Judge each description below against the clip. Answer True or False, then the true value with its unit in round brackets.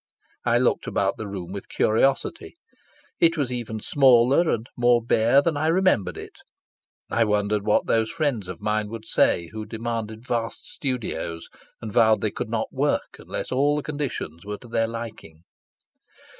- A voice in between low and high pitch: False (115 Hz)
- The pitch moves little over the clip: False (4.0 semitones)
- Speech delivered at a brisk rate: False (165 wpm)